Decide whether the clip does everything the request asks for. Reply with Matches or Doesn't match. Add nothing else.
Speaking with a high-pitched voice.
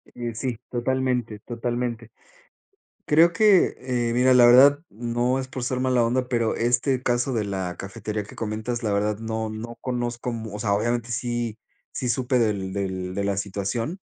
Doesn't match